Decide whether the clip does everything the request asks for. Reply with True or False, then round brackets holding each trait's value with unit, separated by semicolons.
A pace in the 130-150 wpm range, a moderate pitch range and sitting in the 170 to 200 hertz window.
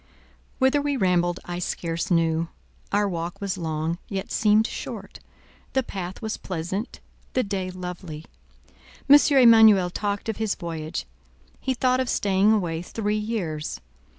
True (135 wpm; 4.2 semitones; 190 Hz)